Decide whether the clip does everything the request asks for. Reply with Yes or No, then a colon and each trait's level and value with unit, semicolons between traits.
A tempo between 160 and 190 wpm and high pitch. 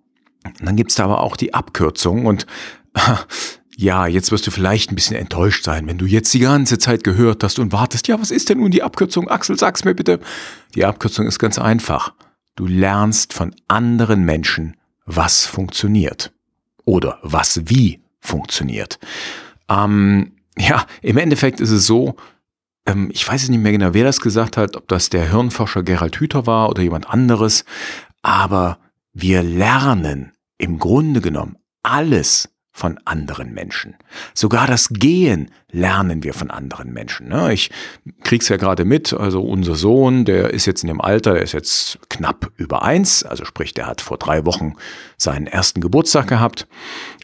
No: average, 170 wpm; low, 105 Hz